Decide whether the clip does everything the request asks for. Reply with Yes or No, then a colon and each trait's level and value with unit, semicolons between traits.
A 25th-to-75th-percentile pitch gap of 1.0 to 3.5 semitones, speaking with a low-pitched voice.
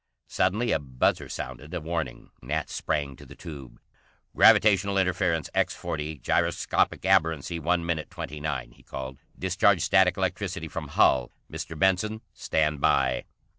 No: average, 4.1 semitones; very low, 80 Hz